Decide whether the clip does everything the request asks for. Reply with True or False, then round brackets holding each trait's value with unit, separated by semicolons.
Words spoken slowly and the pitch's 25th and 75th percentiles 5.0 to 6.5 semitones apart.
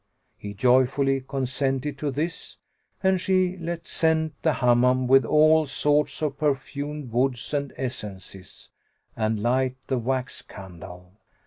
False (125 wpm; 3.5 semitones)